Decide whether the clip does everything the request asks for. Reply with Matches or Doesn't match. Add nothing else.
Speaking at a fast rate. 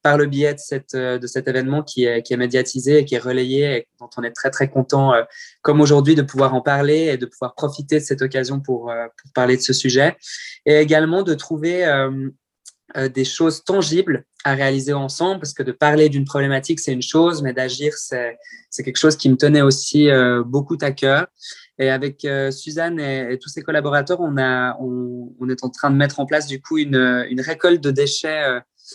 Matches